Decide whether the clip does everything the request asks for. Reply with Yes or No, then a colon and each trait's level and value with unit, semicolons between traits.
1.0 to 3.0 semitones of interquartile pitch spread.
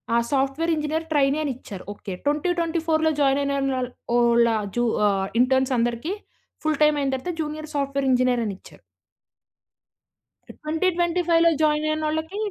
No: average, 3.4 semitones